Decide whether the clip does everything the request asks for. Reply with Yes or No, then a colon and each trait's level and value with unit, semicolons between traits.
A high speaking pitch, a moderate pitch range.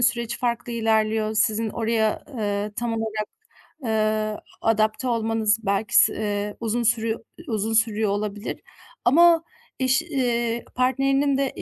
No: high, 225 Hz; narrow, 1.9 semitones